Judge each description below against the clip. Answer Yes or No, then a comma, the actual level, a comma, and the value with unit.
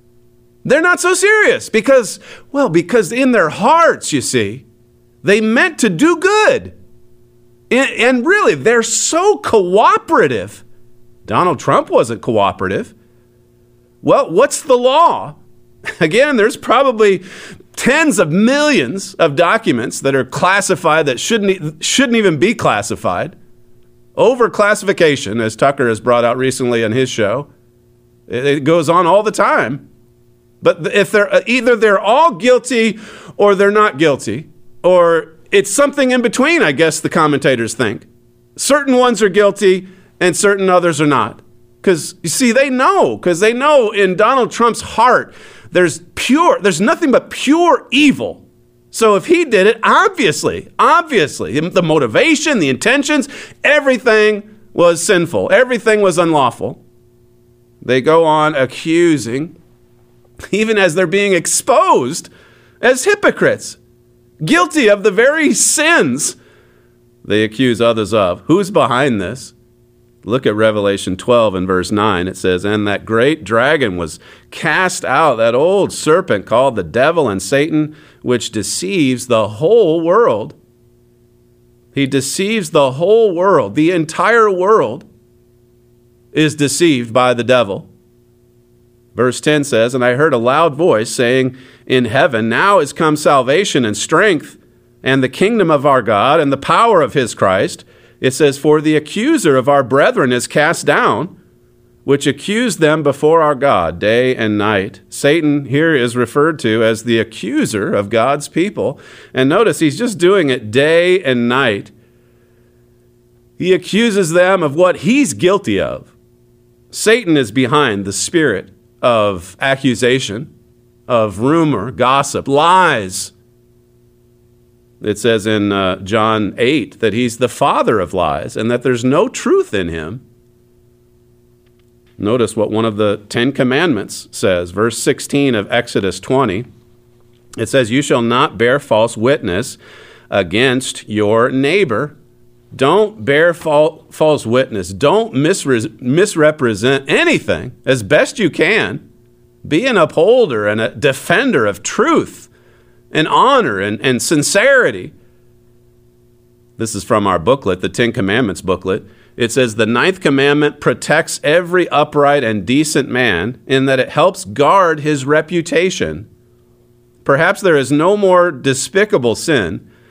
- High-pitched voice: No, low, 135 Hz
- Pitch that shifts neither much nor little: No, wide, 8.0 semitones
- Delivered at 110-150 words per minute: Yes, slow, 135 wpm